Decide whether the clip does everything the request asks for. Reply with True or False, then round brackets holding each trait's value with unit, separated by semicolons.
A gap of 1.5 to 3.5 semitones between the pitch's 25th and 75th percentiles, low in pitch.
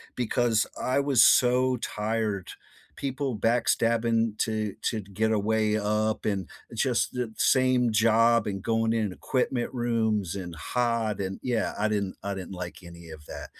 True (2.7 semitones; 110 Hz)